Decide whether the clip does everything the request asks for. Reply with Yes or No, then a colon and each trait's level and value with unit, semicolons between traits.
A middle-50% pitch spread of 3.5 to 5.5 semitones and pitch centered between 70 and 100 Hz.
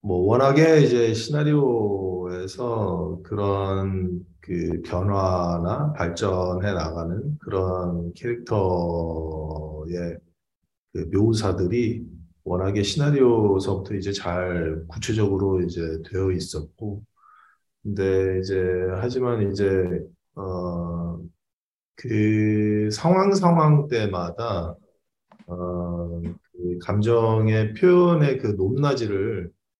Yes: average, 3.8 semitones; very low, 95 Hz